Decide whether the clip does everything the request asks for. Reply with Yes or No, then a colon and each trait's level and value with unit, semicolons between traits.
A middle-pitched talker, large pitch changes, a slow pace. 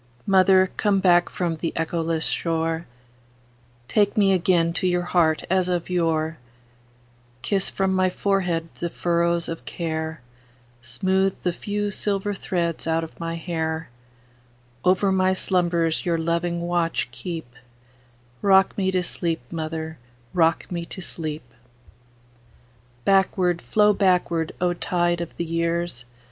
Yes: medium, 165 Hz; wide, 6.6 semitones; slow, 115 wpm